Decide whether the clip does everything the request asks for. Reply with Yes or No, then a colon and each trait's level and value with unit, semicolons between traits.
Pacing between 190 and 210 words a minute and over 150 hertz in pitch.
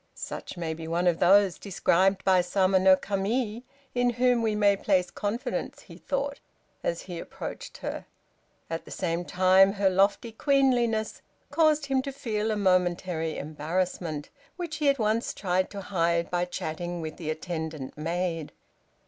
No: average, 155 wpm; high, 190 Hz